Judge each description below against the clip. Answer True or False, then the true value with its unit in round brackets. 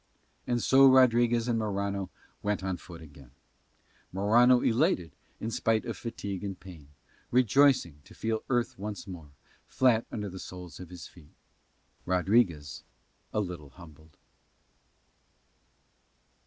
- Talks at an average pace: False (130 wpm)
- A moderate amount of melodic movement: True (5.0 semitones)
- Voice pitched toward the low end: True (100 Hz)